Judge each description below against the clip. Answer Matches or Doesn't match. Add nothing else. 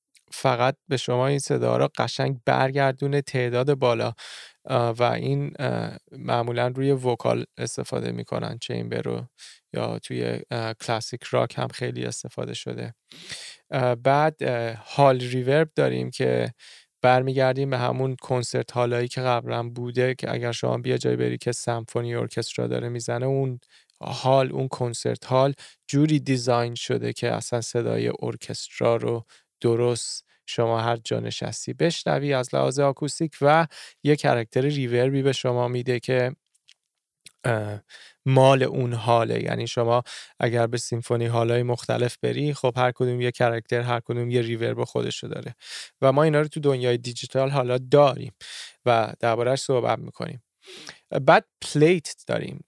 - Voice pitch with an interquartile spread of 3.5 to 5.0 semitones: Doesn't match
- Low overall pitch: Matches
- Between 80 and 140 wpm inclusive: Matches